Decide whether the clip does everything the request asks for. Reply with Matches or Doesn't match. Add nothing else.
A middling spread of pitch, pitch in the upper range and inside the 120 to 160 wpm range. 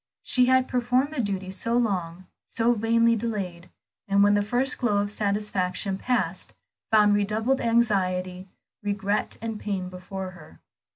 Matches